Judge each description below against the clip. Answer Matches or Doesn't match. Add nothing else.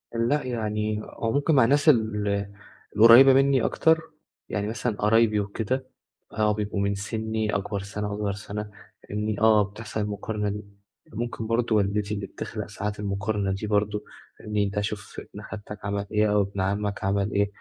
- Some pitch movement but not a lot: Doesn't match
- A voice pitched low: Matches